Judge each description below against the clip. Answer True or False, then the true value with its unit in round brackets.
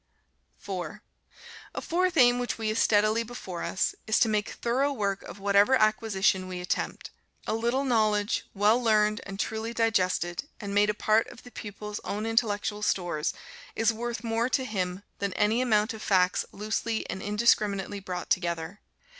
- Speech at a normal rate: True (165 wpm)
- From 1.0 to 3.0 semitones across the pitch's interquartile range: True (2.5 semitones)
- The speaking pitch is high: True (210 Hz)